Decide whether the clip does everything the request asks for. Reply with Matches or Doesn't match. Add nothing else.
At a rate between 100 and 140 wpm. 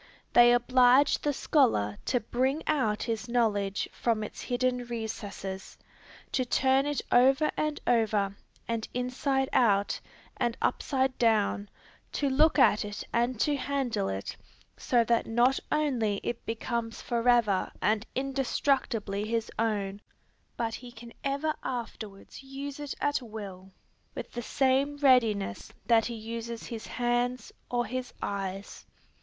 Matches